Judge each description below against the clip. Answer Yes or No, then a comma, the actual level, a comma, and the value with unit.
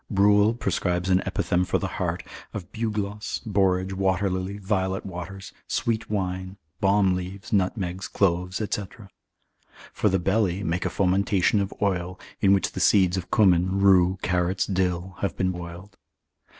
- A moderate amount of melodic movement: No, narrow, 1.6 semitones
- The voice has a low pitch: Yes, very low, 95 Hz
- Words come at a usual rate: Yes, average, 150 wpm